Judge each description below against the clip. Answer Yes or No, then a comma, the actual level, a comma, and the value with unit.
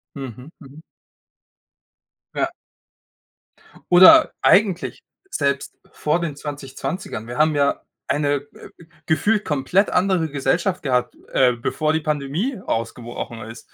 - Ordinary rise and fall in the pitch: Yes, average, 5.0 semitones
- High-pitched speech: No, medium, 150 Hz